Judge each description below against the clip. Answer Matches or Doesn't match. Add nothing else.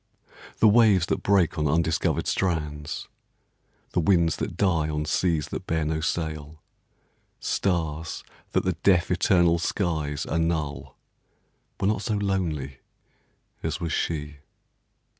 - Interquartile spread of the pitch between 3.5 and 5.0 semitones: Doesn't match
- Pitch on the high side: Doesn't match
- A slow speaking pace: Matches